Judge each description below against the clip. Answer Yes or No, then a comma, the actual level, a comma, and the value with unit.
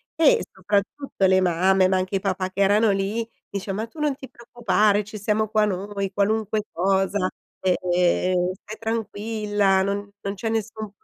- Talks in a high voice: Yes, high, 200 Hz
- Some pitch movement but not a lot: No, narrow, 2.3 semitones